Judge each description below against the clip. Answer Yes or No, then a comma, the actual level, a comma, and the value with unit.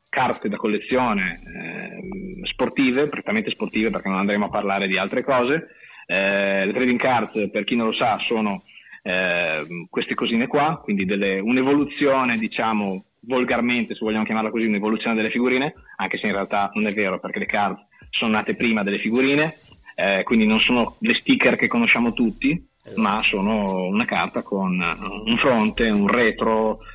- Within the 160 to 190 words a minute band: Yes, average, 165 wpm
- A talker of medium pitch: No, low, 115 Hz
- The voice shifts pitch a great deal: Yes, wide, 6.4 semitones